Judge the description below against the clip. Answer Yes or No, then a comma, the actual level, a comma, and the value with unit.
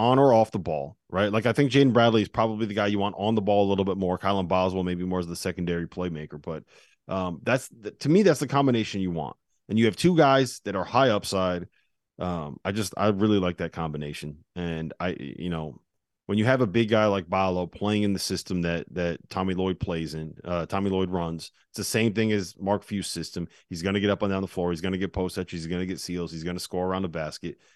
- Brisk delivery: Yes, fast, 260 wpm